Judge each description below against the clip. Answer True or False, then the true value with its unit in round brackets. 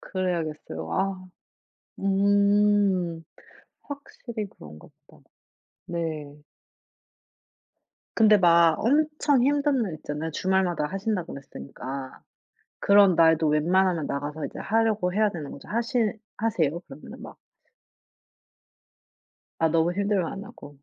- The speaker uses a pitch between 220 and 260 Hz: False (185 Hz)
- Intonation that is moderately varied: True (4.6 semitones)